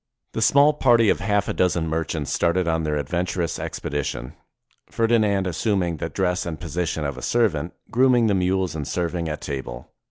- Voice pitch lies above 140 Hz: No, very low, 90 Hz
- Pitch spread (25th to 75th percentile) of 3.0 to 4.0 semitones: No, average, 4.4 semitones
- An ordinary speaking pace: Yes, average, 170 wpm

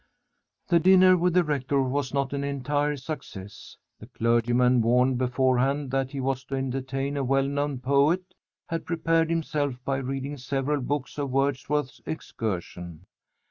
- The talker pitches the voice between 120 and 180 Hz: Yes, low, 135 Hz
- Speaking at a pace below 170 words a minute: Yes, average, 145 wpm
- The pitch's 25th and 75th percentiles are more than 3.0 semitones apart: No, narrow, 2.4 semitones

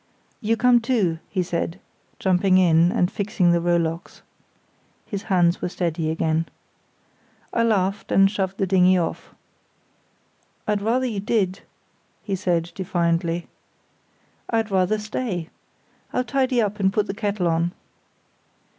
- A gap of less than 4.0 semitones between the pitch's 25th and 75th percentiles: Yes, average, 3.4 semitones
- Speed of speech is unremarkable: No, slow, 130 wpm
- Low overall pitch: No, high, 190 Hz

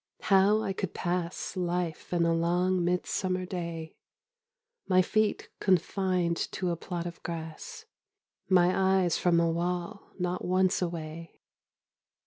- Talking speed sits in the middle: No, slow, 125 wpm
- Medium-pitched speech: Yes, medium, 180 Hz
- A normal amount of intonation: No, narrow, 1.8 semitones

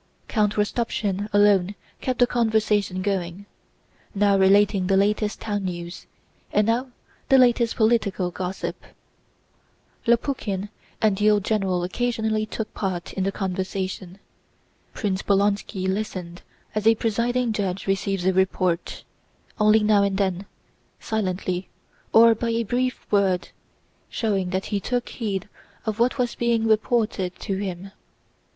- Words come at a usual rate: No, slow, 130 wpm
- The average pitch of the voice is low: No, high, 205 Hz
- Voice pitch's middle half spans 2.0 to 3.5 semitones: Yes, average, 2.7 semitones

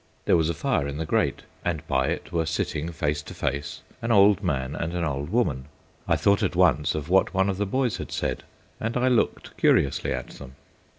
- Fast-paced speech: Yes, fast, 220 wpm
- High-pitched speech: No, very low, 85 Hz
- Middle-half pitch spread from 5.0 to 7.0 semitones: Yes, wide, 5.5 semitones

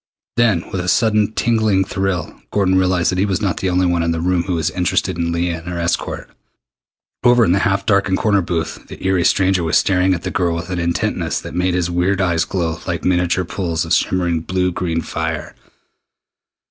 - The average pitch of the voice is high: No, very low, 90 Hz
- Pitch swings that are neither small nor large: No, narrow, 2.1 semitones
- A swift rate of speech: Yes, fast, 210 wpm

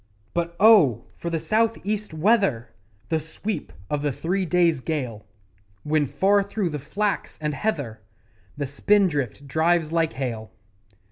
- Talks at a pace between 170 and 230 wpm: No, average, 140 wpm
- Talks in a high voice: No, medium, 160 Hz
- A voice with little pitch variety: No, wide, 5.6 semitones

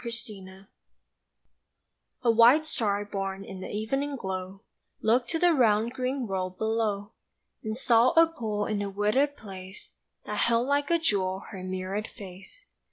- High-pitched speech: Yes, high, 215 Hz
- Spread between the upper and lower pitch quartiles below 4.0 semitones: No, average, 4.5 semitones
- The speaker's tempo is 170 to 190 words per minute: No, average, 155 wpm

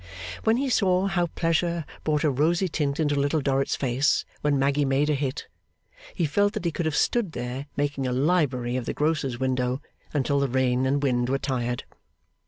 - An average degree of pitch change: Yes, average, 3.7 semitones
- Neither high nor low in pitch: Yes, medium, 145 Hz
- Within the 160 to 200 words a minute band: Yes, average, 190 wpm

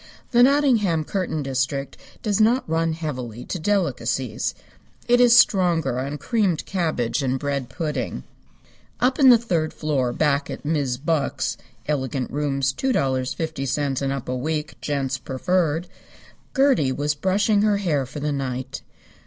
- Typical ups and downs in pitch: No, wide, 5.8 semitones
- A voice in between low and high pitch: Yes, medium, 150 Hz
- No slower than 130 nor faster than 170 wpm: Yes, average, 140 wpm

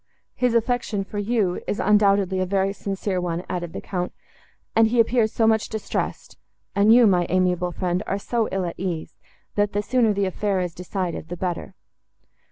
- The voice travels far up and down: No, average, 3.2 semitones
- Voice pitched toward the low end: No, high, 195 Hz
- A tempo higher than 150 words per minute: Yes, average, 175 wpm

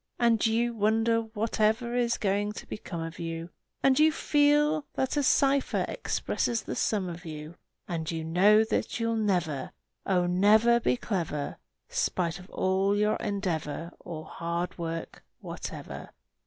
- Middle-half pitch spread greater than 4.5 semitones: Yes, average, 5.3 semitones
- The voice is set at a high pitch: Yes, high, 205 Hz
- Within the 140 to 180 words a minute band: Yes, average, 150 wpm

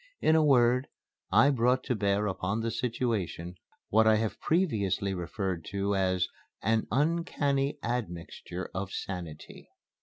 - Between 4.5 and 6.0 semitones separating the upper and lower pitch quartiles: Yes, average, 5.1 semitones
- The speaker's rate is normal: No, slow, 130 wpm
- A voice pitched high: No, low, 110 Hz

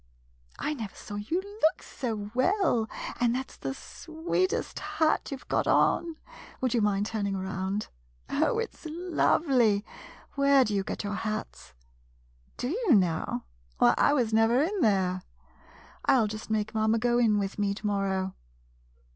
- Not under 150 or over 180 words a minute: Yes, average, 160 wpm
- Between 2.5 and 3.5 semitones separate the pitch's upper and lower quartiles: No, wide, 5.6 semitones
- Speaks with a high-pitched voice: Yes, high, 220 Hz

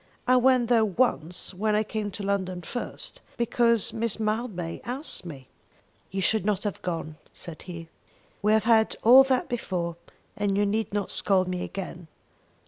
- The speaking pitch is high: Yes, high, 205 Hz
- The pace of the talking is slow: No, average, 165 wpm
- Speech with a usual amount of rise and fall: Yes, average, 4.2 semitones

